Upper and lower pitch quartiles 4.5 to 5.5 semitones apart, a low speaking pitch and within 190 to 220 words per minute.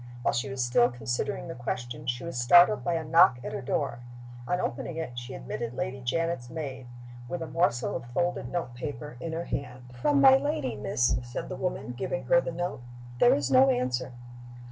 Yes: average, 4.9 semitones; low, 130 Hz; average, 200 wpm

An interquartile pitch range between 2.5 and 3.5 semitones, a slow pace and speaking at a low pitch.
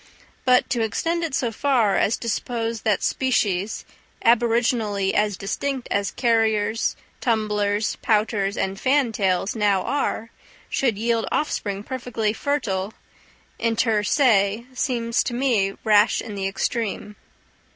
No: average, 2.9 semitones; slow, 120 wpm; high, 225 Hz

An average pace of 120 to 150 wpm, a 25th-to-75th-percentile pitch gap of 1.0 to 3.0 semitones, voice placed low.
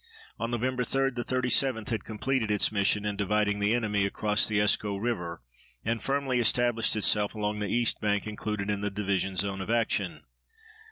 No: average, 175 wpm; average, 2.7 semitones; low, 105 Hz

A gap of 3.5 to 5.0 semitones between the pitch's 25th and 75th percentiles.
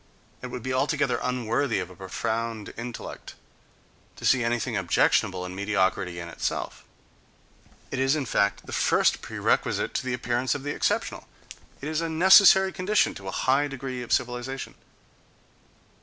Yes: average, 4.4 semitones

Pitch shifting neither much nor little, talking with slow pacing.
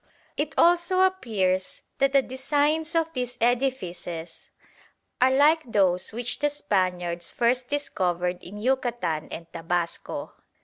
No: wide, 8.2 semitones; slow, 120 wpm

